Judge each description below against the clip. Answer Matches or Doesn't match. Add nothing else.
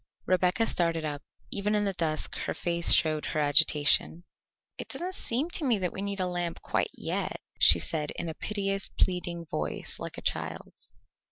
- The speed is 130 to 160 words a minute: Doesn't match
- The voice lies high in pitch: Doesn't match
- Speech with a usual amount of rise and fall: Matches